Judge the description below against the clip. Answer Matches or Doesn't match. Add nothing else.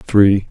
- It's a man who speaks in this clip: Matches